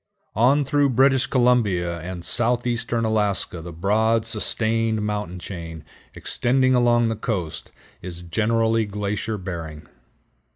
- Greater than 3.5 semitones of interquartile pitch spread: Yes, average, 4.7 semitones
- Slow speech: Yes, slow, 115 wpm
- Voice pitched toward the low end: Yes, low, 110 Hz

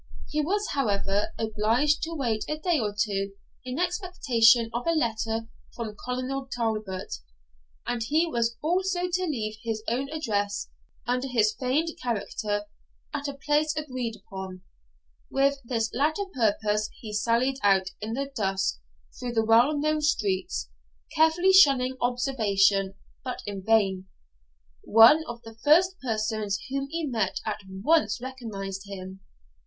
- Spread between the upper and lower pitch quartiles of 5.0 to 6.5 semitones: Yes, wide, 5.4 semitones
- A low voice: No, high, 235 Hz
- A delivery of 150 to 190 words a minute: No, average, 140 wpm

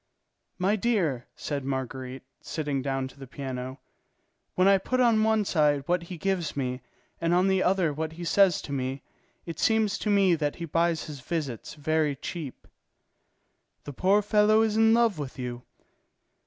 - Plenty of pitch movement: Yes, wide, 6.0 semitones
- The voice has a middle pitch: Yes, medium, 165 Hz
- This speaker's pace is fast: No, average, 170 wpm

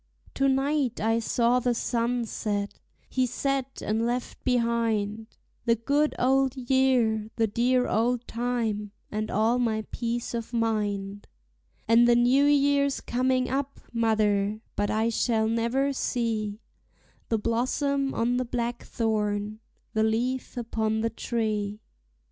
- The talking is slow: Yes, slow, 130 wpm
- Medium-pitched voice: No, high, 235 Hz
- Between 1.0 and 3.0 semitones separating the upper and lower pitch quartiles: Yes, narrow, 2.5 semitones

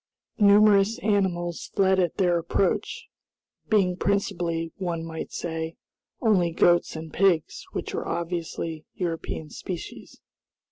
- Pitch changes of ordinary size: Yes, average, 3.0 semitones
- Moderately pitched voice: Yes, medium, 175 Hz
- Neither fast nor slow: No, slow, 110 wpm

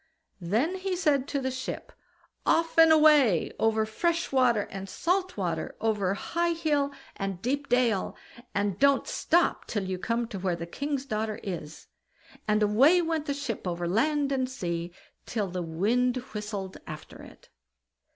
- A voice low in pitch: No, high, 235 Hz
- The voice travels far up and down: Yes, wide, 6.9 semitones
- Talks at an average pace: Yes, average, 160 wpm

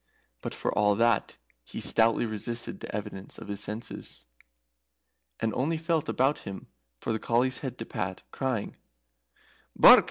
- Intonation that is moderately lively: Yes, average, 3.9 semitones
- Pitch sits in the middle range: No, low, 115 Hz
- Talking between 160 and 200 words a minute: No, average, 150 wpm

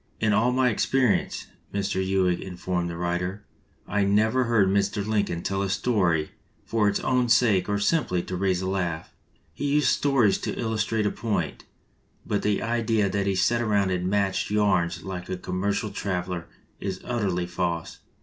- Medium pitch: No, low, 100 Hz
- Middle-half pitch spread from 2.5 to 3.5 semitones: Yes, average, 3.0 semitones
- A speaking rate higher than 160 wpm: Yes, average, 170 wpm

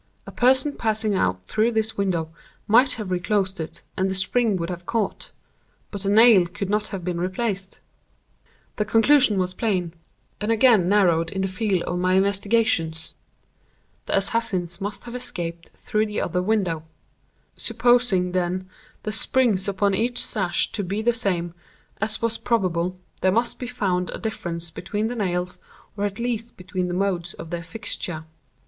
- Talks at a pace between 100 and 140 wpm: No, average, 165 wpm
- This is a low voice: No, high, 195 Hz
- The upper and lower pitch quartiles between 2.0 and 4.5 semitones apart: Yes, average, 3.6 semitones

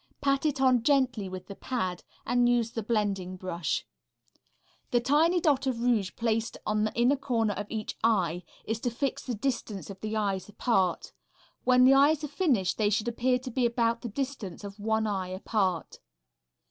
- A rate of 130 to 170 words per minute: No, average, 185 wpm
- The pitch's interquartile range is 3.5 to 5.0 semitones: Yes, average, 4.1 semitones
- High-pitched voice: Yes, high, 230 Hz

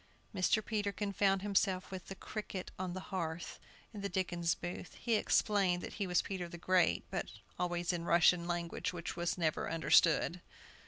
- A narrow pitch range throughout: Yes, narrow, 2.2 semitones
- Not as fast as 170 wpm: No, average, 175 wpm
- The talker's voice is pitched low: No, medium, 180 Hz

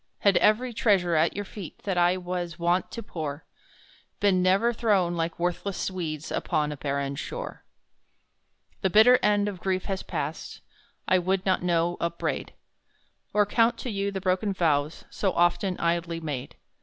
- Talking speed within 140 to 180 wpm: Yes, average, 160 wpm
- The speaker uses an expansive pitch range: No, average, 3.1 semitones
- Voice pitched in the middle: Yes, medium, 180 Hz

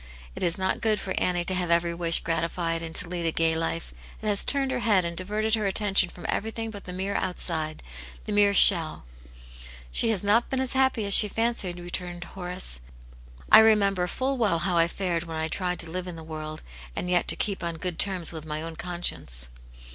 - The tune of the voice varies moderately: Yes, average, 3.5 semitones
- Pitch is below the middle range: No, medium, 180 Hz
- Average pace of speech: No, fast, 230 wpm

